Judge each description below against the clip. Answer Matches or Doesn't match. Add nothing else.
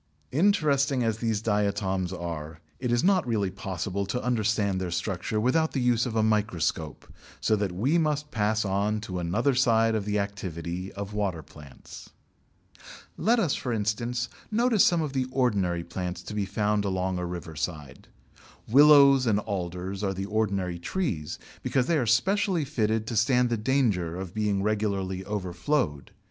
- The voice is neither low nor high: Doesn't match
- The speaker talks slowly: Doesn't match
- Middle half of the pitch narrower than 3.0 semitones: Doesn't match